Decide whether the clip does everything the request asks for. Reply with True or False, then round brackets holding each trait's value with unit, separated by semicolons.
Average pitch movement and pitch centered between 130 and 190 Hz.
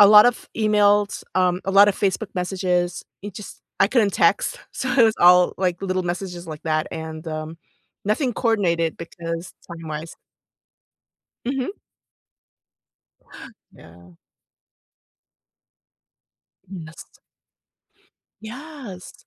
True (3.9 semitones; 185 Hz)